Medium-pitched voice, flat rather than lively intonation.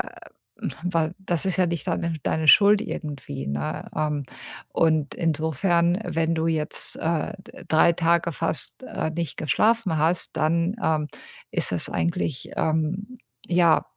Yes: medium, 165 Hz; narrow, 1.9 semitones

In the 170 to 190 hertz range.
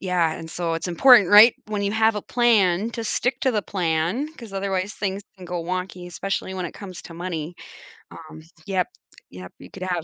Yes: medium, 185 Hz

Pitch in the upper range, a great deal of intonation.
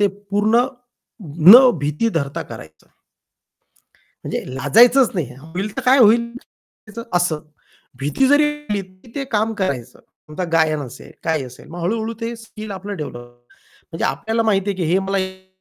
Yes: high, 195 Hz; wide, 6.2 semitones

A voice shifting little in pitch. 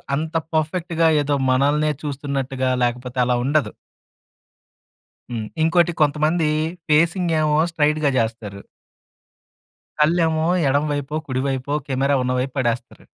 No: average, 3.2 semitones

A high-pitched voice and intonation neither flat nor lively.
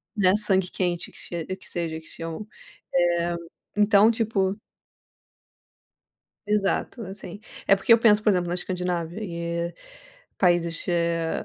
No: medium, 180 Hz; average, 3.3 semitones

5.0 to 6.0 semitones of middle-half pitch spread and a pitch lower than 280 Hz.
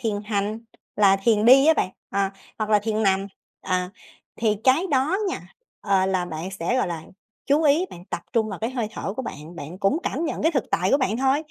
Yes: average, 5.3 semitones; high, 215 Hz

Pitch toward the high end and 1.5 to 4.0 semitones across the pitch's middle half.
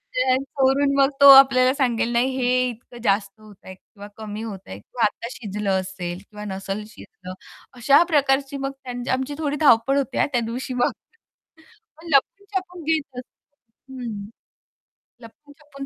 No: very high, 255 Hz; average, 4.4 semitones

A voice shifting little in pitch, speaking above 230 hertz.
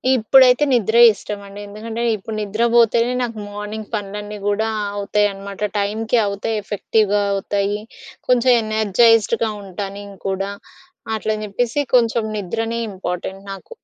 No: narrow, 2.2 semitones; high, 210 Hz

